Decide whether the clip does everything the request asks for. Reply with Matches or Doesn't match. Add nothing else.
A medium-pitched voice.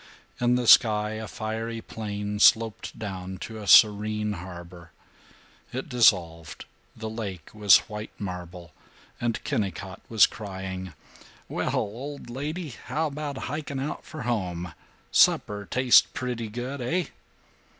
Doesn't match